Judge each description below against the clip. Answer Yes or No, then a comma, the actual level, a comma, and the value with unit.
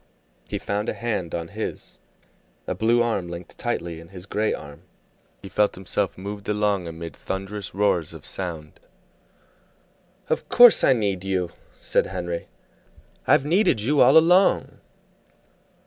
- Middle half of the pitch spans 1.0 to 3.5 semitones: No, average, 4.1 semitones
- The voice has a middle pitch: No, very low, 95 Hz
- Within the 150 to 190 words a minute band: No, average, 140 wpm